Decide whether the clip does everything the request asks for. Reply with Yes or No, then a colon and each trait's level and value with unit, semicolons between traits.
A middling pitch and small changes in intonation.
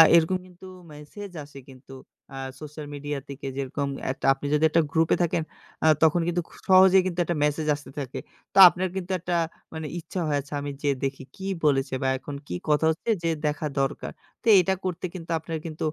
No: medium, 155 Hz; average, 3.4 semitones